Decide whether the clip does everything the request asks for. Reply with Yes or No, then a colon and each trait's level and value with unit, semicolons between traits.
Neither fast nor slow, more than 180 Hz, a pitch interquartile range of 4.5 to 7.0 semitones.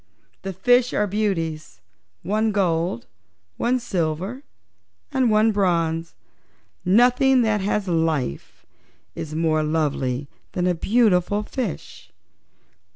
No: slow, 100 wpm; high, 190 Hz; average, 5.1 semitones